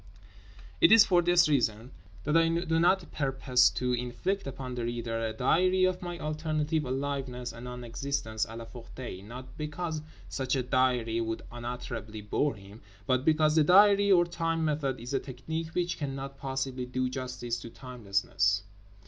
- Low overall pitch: Yes, low, 130 Hz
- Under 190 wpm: Yes, average, 165 wpm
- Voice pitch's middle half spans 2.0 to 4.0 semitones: No, average, 4.8 semitones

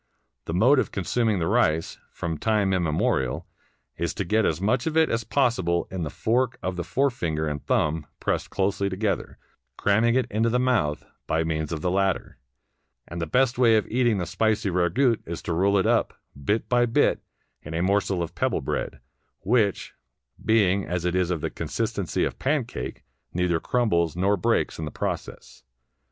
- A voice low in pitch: Yes, very low, 95 Hz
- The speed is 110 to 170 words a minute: No, average, 180 wpm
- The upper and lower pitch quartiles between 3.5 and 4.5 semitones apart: No, wide, 5.4 semitones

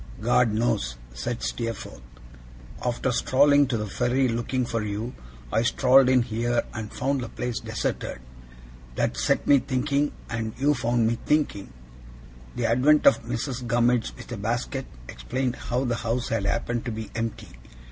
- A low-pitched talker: Yes, low, 120 Hz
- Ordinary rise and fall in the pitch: No, narrow, 2.2 semitones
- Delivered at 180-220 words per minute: No, average, 155 wpm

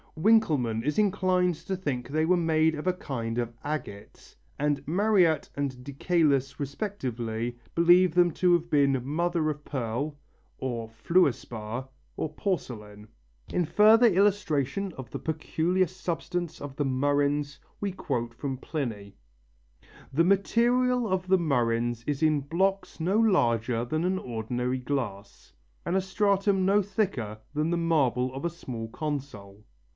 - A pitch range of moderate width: No, wide, 6.5 semitones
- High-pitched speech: No, medium, 150 Hz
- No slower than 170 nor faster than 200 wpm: No, average, 145 wpm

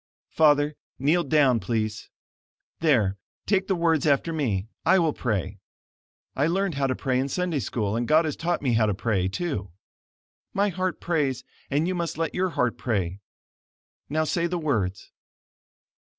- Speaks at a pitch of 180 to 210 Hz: No, medium, 145 Hz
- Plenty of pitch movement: Yes, wide, 6.9 semitones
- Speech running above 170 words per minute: No, average, 165 wpm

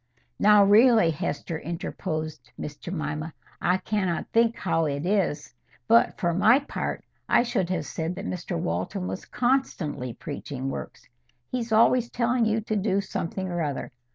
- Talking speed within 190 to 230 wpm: No, average, 155 wpm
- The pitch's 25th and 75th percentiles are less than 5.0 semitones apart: No, wide, 5.6 semitones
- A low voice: No, medium, 185 Hz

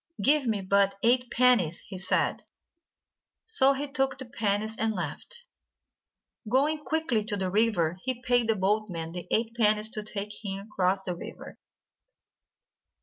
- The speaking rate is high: No, average, 145 wpm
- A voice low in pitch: No, high, 215 Hz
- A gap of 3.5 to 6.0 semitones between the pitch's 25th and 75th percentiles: Yes, average, 4.4 semitones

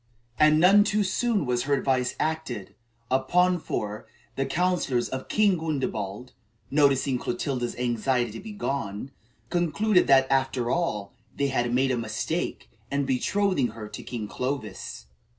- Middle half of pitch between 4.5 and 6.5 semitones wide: Yes, wide, 5.4 semitones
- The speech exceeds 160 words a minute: No, average, 140 wpm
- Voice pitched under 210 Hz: Yes, low, 135 Hz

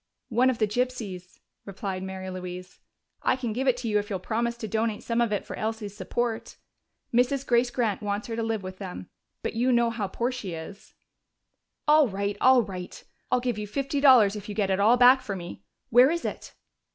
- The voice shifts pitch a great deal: No, average, 3.7 semitones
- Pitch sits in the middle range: No, high, 225 Hz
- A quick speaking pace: Yes, fast, 215 wpm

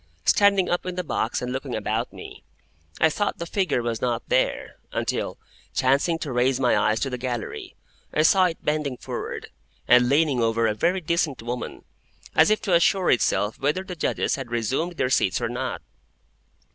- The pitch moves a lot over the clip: Yes, wide, 5.8 semitones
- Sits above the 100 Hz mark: Yes, low, 135 Hz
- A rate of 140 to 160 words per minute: No, average, 185 wpm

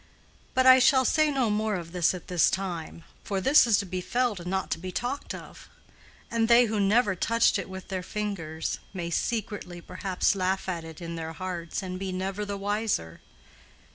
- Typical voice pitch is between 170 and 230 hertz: Yes, high, 190 Hz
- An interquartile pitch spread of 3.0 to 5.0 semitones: Yes, average, 3.6 semitones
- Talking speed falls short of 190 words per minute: No, average, 200 wpm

